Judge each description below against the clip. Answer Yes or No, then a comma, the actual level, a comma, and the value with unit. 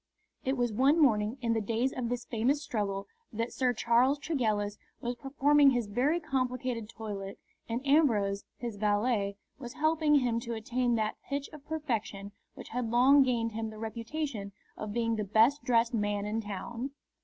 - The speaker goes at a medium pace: Yes, average, 170 wpm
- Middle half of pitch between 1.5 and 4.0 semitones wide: Yes, average, 3.7 semitones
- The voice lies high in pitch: Yes, high, 235 Hz